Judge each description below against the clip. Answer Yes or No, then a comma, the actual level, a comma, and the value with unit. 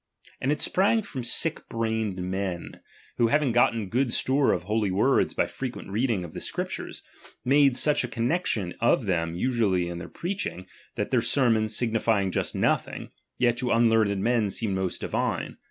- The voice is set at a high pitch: No, low, 115 Hz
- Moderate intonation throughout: Yes, average, 4.6 semitones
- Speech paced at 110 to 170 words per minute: No, average, 185 wpm